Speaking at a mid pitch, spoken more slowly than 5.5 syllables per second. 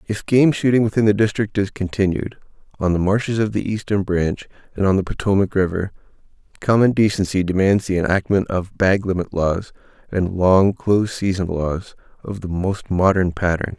No: low, 100 Hz; 5.1 syllables/s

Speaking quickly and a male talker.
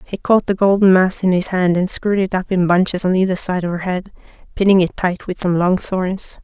No: fast, 250 wpm; female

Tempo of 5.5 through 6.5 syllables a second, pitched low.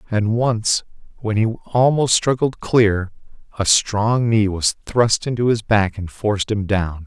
No: 3.9 syllables/s; low, 110 Hz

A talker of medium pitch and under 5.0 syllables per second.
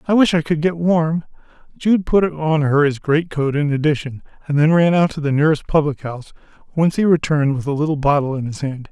No: medium, 155 Hz; 6.0 syllables/s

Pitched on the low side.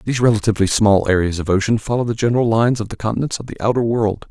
Yes: low, 110 Hz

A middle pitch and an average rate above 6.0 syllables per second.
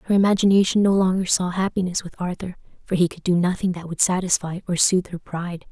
Yes: medium, 180 Hz; 6.4 syllables/s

